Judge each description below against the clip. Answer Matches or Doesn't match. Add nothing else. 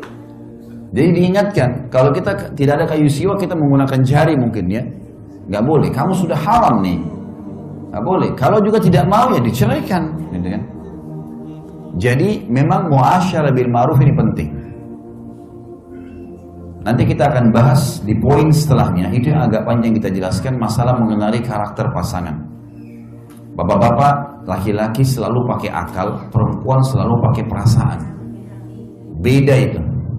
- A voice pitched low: Matches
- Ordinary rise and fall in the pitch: Doesn't match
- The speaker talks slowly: Doesn't match